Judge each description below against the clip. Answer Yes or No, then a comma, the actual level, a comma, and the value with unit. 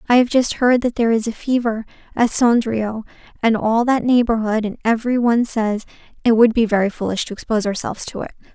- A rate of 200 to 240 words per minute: Yes, fast, 205 wpm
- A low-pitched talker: No, high, 230 Hz